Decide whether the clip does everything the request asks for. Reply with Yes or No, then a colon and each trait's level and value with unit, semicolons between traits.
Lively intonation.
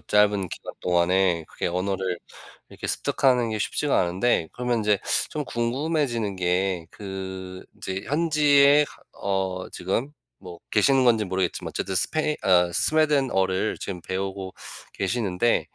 No: average, 5.0 semitones